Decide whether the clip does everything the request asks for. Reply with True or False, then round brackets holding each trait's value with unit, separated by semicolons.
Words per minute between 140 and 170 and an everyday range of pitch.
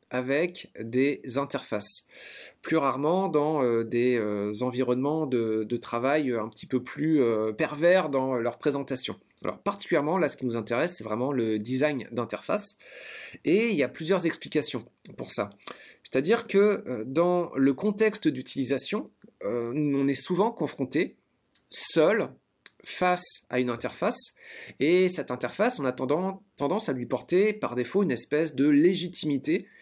False (150 wpm; 5.7 semitones)